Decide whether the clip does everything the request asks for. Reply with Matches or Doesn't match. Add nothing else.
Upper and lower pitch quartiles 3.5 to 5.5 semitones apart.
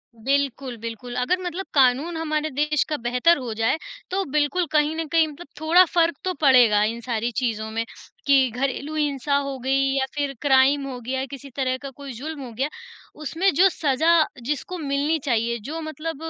Matches